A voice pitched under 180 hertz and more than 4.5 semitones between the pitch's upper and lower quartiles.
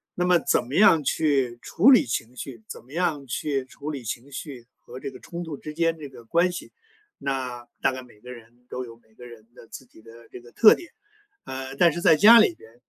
Yes: low, 135 Hz; average, 5.2 semitones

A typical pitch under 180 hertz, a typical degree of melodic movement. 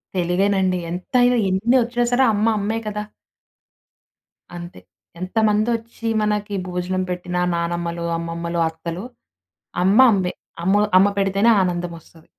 No: high, 190 Hz; average, 3.5 semitones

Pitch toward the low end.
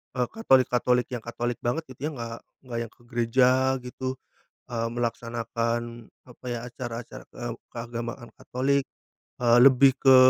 Yes: low, 120 Hz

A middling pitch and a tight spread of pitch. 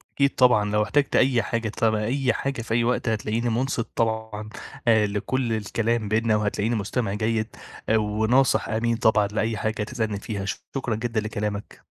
No: low, 110 Hz; narrow, 1.9 semitones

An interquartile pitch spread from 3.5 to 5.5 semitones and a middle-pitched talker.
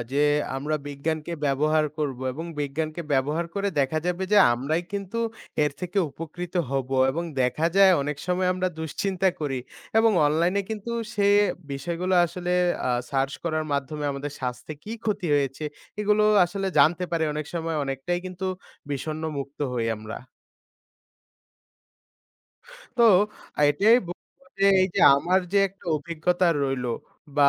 Yes: average, 4.5 semitones; medium, 160 Hz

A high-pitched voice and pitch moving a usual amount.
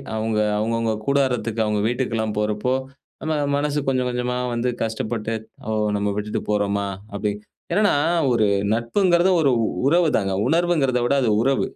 No: low, 115 Hz; average, 4.5 semitones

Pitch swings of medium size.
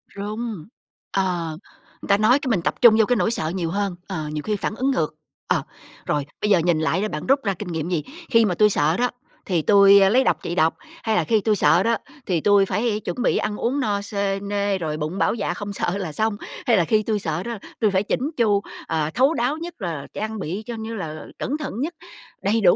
Yes: average, 4.1 semitones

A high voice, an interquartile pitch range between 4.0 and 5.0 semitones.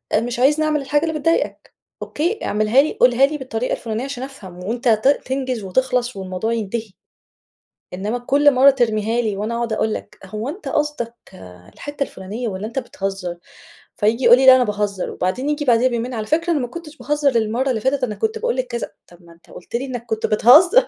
Yes: high, 240 Hz; average, 4.6 semitones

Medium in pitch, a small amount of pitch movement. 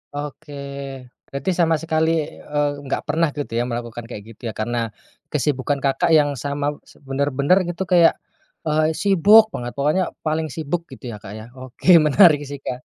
No: medium, 145 Hz; average, 3.7 semitones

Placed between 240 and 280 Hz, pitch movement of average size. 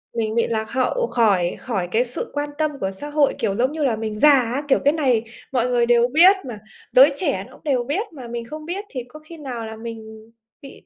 Yes: high, 245 Hz; average, 4.4 semitones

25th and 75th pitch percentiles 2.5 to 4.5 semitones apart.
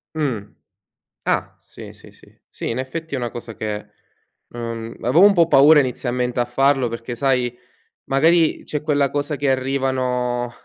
Yes: average, 2.9 semitones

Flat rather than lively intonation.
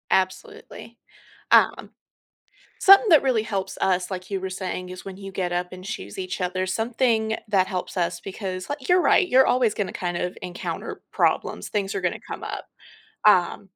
No: average, 3.3 semitones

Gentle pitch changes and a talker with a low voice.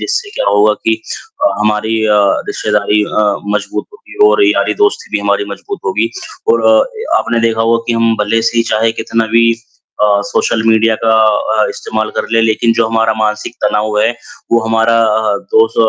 Yes: narrow, 1.4 semitones; low, 115 Hz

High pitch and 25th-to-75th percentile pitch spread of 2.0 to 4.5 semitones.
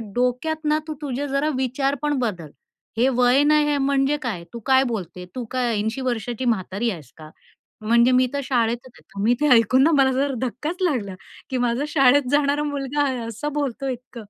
Yes: very high, 255 Hz; average, 3.3 semitones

